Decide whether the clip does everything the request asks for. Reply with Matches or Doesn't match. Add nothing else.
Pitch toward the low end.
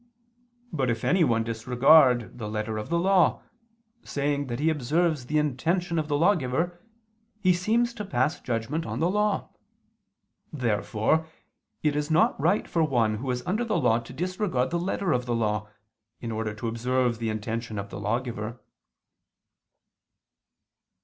Matches